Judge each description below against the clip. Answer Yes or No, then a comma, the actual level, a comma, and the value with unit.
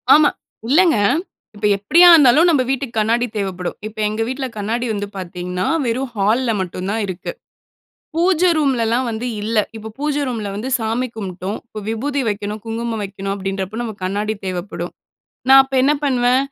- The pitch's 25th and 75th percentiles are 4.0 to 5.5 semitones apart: Yes, average, 4.5 semitones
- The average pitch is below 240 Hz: Yes, high, 225 Hz